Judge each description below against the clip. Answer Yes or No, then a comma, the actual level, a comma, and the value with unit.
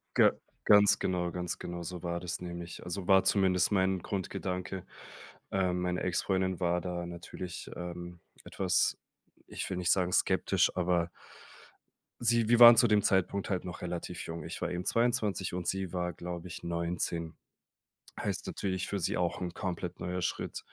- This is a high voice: No, very low, 90 Hz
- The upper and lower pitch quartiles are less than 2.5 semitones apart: Yes, narrow, 1.5 semitones